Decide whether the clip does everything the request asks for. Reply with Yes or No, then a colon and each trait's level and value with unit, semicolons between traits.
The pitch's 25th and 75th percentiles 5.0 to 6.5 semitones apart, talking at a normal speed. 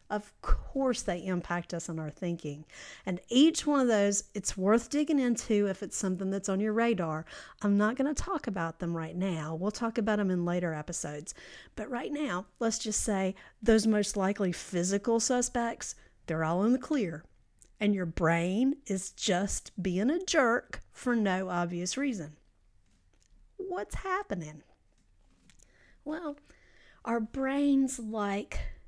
Yes: wide, 5.6 semitones; average, 155 wpm